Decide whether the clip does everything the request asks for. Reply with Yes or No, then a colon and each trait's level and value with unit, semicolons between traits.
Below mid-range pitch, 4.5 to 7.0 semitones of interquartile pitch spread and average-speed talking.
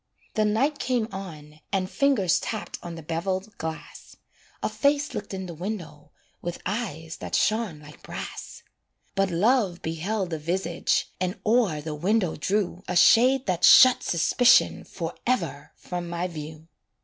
No: medium, 185 Hz; average, 5.0 semitones; average, 150 wpm